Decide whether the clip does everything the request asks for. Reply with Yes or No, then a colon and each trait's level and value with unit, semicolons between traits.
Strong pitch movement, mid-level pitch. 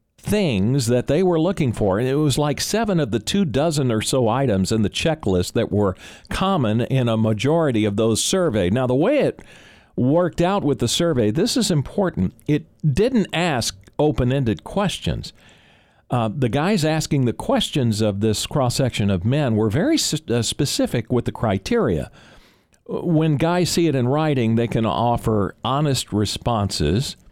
No: wide, 6.0 semitones; low, 130 Hz